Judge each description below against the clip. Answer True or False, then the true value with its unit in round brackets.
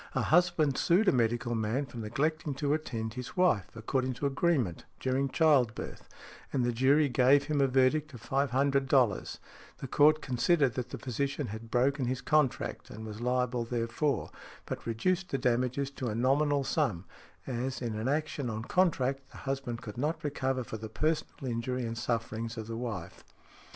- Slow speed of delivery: False (175 wpm)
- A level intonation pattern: False (3.5 semitones)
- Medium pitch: False (130 Hz)